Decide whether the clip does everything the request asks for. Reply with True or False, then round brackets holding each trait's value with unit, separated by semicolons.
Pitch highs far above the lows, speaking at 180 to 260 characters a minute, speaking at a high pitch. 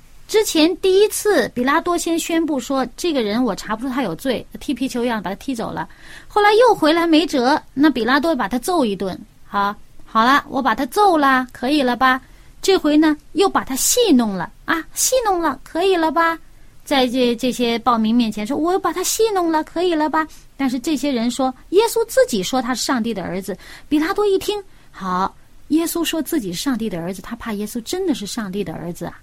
False (5.8 semitones; 300 characters per minute; 275 Hz)